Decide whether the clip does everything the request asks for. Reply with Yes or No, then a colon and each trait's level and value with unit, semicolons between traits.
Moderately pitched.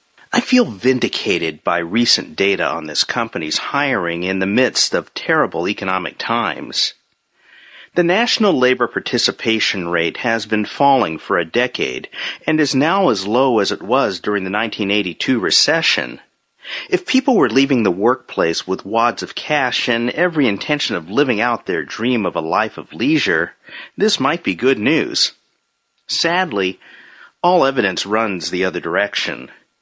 No: low, 115 Hz